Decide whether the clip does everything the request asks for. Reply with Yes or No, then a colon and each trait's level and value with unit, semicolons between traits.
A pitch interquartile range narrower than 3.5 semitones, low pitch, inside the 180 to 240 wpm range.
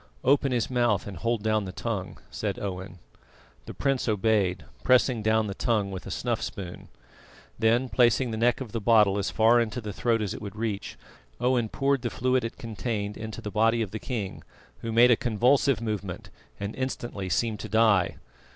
Yes: average, 2.9 semitones; low, 110 Hz; average, 190 wpm